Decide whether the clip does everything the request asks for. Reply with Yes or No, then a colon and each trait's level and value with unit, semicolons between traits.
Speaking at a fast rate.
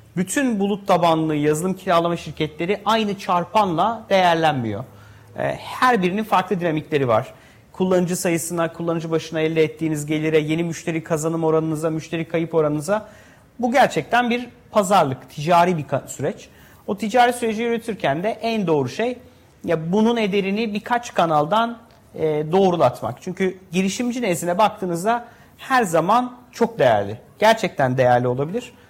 No: average, 125 wpm